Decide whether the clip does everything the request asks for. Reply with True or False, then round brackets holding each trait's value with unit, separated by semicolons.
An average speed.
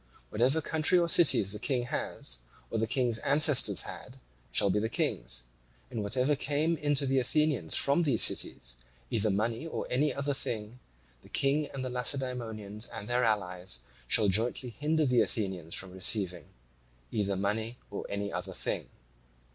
True (165 wpm)